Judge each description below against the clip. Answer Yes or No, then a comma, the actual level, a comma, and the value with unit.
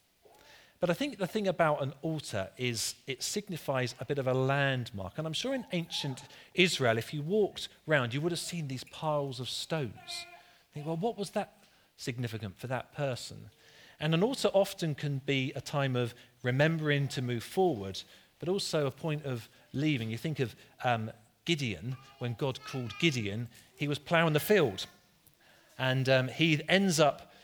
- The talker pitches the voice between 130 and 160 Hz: Yes, medium, 140 Hz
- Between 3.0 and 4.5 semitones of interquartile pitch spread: No, average, 4.9 semitones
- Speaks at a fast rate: No, average, 180 wpm